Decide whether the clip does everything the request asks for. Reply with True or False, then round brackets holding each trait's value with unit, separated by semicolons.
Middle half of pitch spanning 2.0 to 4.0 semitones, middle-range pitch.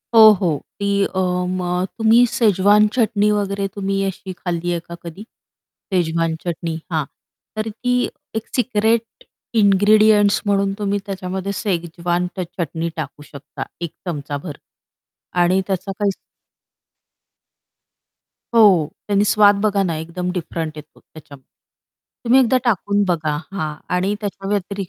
False (3.3 semitones; 195 Hz)